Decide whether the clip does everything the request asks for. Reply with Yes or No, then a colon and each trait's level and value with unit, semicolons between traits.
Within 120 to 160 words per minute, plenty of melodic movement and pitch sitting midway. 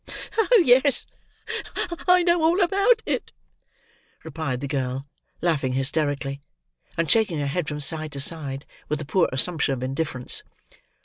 Yes: average, 140 wpm; wide, 8.5 semitones; medium, 155 Hz